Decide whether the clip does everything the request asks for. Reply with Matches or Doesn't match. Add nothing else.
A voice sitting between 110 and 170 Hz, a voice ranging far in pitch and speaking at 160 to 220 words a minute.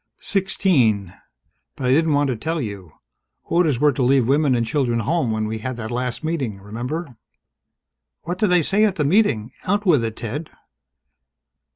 Matches